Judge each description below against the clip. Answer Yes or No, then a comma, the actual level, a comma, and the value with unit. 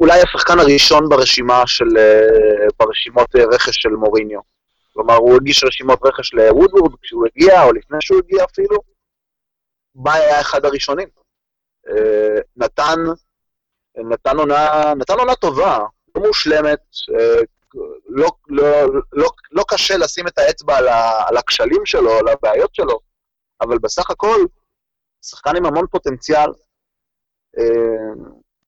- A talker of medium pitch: Yes, medium, 165 Hz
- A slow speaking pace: No, average, 120 wpm